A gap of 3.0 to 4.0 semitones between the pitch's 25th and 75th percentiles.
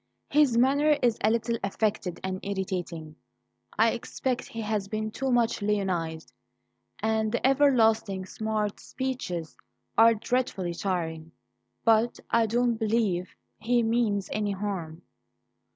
Yes: average, 3.7 semitones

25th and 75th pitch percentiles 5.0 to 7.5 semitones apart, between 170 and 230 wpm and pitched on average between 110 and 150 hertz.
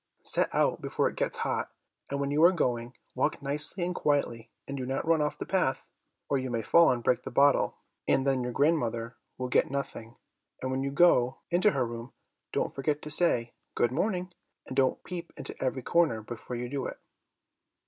No: average, 3.8 semitones; average, 200 wpm; low, 135 Hz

